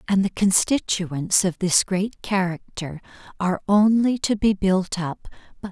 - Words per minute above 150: No, average, 145 wpm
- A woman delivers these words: Yes, female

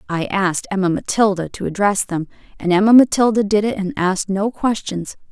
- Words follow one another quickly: No, average, 180 wpm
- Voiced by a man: No, female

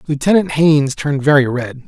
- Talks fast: No, average, 160 wpm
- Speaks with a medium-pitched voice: Yes, medium, 145 Hz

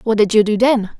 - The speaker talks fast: Yes, fast, 300 wpm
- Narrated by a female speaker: Yes, female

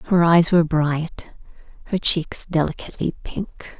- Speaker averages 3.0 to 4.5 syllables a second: Yes, 4.2 syllables/s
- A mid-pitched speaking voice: Yes, medium, 165 Hz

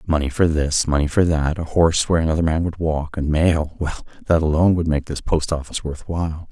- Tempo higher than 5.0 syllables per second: Yes, 6.0 syllables/s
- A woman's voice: No, male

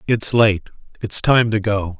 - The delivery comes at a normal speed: Yes, average, 180 wpm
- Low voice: Yes, low, 105 Hz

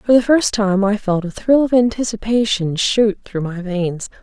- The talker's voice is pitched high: Yes, high, 210 Hz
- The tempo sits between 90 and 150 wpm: No, average, 200 wpm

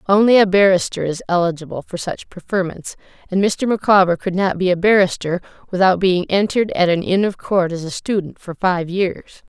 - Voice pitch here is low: No, medium, 185 Hz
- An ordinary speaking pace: Yes, average, 190 wpm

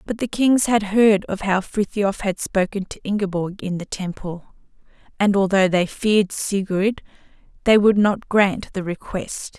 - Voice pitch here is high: Yes, high, 200 Hz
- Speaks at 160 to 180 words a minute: Yes, average, 165 wpm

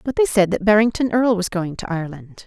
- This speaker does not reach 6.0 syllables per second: No, 6.3 syllables/s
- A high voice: Yes, high, 200 Hz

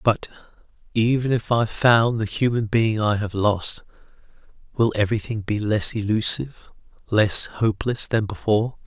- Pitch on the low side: Yes, low, 110 Hz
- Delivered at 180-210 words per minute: No, slow, 135 wpm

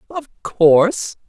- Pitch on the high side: Yes, high, 210 Hz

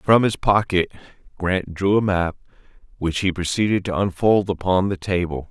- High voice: No, very low, 95 Hz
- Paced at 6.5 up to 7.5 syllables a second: No, 4.9 syllables/s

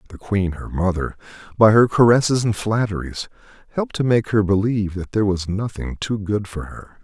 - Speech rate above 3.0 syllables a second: Yes, 5.7 syllables/s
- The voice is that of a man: Yes, male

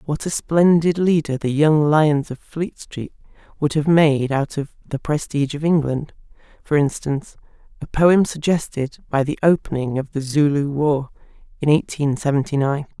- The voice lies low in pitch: No, medium, 150 Hz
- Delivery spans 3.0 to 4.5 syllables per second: No, 4.7 syllables/s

